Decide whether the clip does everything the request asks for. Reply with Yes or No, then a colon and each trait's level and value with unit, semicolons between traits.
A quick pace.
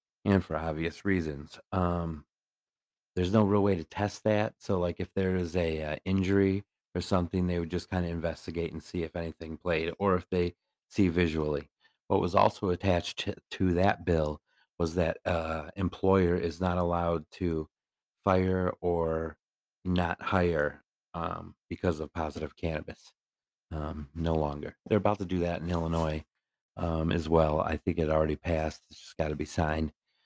No: average, 175 wpm